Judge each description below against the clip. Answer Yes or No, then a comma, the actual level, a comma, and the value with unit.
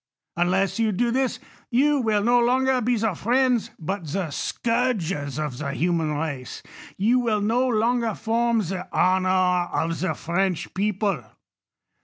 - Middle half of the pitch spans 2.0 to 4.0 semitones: No, average, 5.2 semitones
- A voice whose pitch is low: No, high, 205 Hz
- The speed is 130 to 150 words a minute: Yes, average, 145 wpm